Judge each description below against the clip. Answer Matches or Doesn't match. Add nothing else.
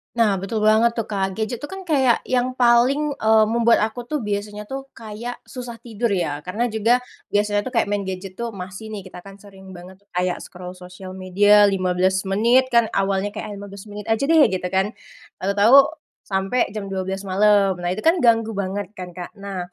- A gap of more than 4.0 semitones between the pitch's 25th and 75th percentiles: Doesn't match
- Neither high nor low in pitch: Doesn't match